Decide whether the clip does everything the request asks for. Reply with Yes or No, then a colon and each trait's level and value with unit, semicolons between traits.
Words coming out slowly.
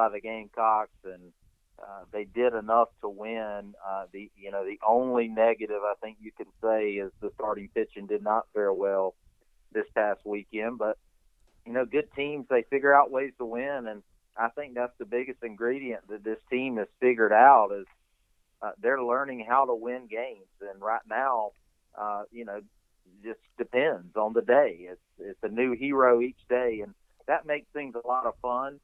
No: average, 190 wpm